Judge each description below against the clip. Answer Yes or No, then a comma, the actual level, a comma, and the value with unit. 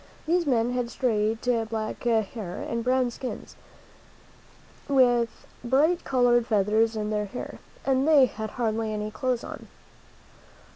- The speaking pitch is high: Yes, high, 235 Hz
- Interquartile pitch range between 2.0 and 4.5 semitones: Yes, average, 2.9 semitones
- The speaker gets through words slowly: Yes, slow, 130 wpm